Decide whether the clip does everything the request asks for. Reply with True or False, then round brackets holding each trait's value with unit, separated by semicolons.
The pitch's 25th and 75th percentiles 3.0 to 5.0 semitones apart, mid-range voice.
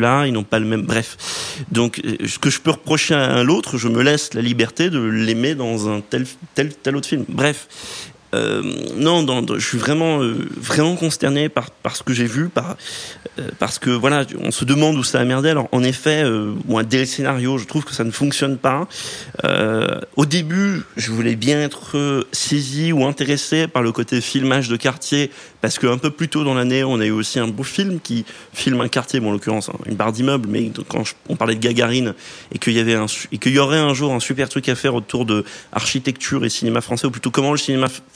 False (3.7 semitones; 130 Hz)